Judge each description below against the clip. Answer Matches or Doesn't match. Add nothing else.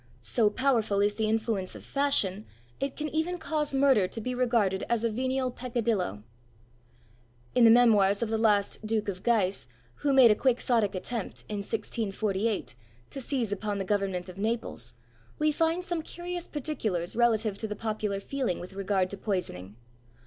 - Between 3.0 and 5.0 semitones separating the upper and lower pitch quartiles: Matches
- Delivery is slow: Doesn't match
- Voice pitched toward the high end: Matches